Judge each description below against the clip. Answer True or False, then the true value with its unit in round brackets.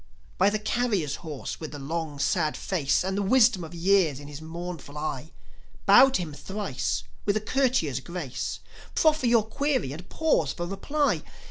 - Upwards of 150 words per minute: True (170 wpm)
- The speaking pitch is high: False (175 Hz)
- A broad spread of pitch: True (6.3 semitones)